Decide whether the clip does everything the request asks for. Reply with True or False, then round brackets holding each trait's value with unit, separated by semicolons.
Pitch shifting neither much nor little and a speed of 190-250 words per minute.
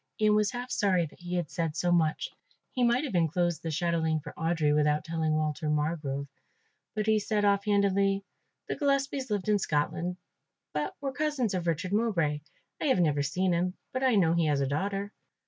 True (5.0 semitones; 195 wpm)